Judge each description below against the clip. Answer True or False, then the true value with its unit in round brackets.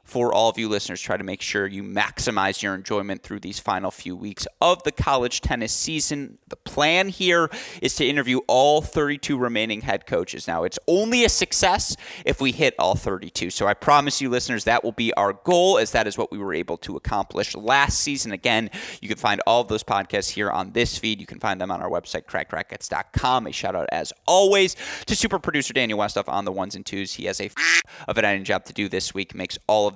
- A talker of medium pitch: False (120 Hz)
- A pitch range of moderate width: False (6.9 semitones)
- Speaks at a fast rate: True (230 wpm)